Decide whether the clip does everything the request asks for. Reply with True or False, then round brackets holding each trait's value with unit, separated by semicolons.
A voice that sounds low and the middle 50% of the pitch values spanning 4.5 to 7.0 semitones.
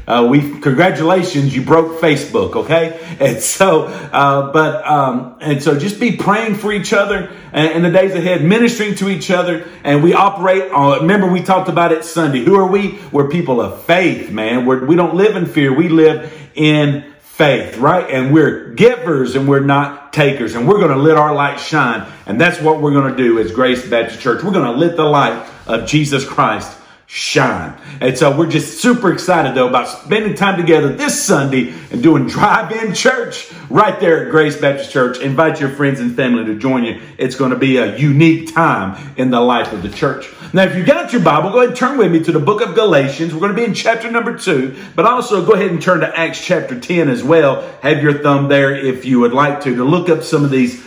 False (155 Hz; 5.2 semitones)